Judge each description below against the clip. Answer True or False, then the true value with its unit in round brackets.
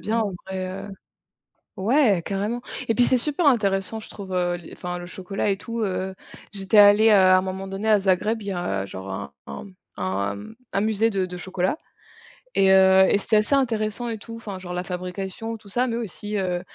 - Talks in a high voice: True (195 Hz)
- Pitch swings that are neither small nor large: True (3.1 semitones)